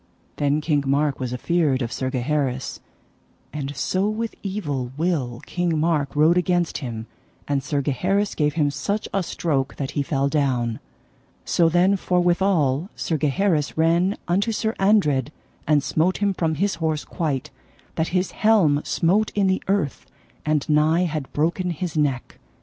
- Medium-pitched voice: Yes, medium, 155 Hz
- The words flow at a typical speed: Yes, average, 155 wpm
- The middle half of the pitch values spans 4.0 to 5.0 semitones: Yes, average, 4.3 semitones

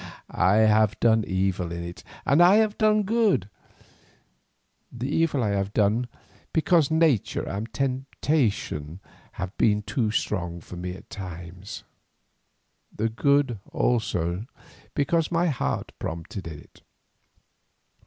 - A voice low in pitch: Yes, low, 110 Hz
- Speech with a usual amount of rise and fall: No, wide, 7.5 semitones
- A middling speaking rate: No, slow, 125 wpm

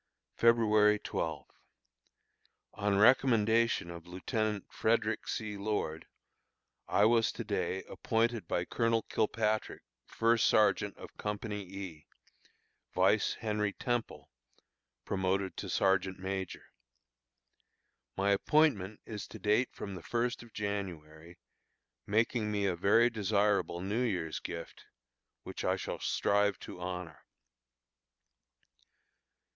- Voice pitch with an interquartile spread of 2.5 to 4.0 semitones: Yes, average, 2.9 semitones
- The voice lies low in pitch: Yes, low, 105 Hz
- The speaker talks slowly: Yes, slow, 110 wpm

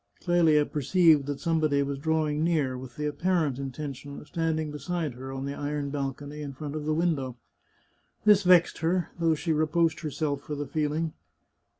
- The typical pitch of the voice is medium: Yes, medium, 150 Hz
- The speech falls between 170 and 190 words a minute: Yes, average, 175 wpm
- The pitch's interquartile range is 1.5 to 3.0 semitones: Yes, narrow, 2.5 semitones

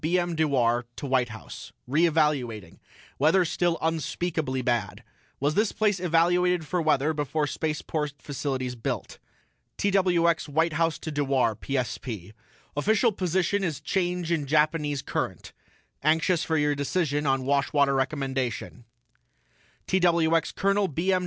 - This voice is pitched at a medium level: Yes, medium, 155 Hz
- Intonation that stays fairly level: No, average, 4.2 semitones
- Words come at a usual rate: No, slow, 130 wpm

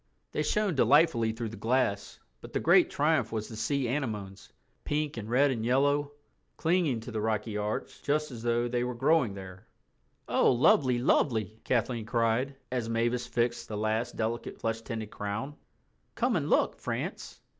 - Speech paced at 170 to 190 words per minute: No, average, 160 wpm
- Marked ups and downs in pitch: No, average, 3.4 semitones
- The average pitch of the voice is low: Yes, low, 120 Hz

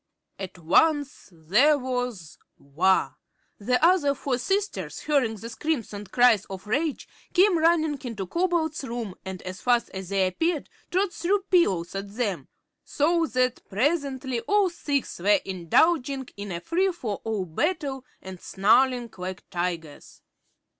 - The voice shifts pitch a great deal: Yes, wide, 8.5 semitones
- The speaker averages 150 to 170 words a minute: No, average, 140 wpm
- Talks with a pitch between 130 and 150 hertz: No, very high, 250 Hz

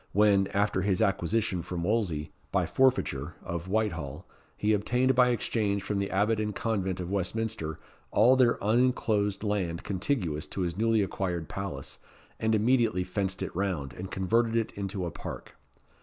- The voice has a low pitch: Yes, low, 100 Hz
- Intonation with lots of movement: No, average, 3.6 semitones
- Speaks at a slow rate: No, average, 155 wpm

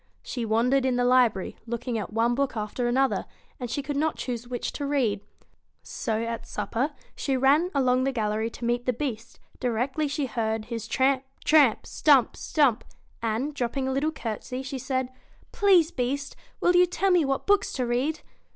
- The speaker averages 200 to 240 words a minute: No, average, 180 wpm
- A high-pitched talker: Yes, very high, 255 Hz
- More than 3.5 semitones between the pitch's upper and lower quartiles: No, average, 3.2 semitones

